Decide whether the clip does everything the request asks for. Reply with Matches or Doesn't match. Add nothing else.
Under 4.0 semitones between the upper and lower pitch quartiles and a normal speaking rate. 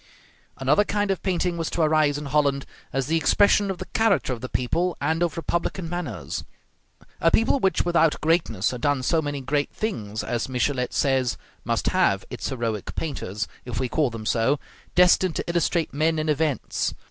Doesn't match